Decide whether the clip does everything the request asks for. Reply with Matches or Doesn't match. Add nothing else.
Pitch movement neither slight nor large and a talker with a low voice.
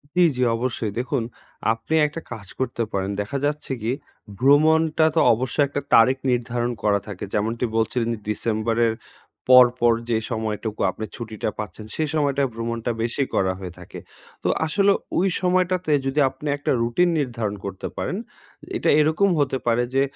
Matches